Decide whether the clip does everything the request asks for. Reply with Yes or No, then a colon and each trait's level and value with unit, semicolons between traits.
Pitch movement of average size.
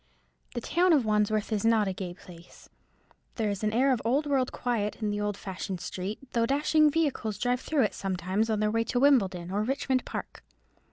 Yes: average, 4.2 semitones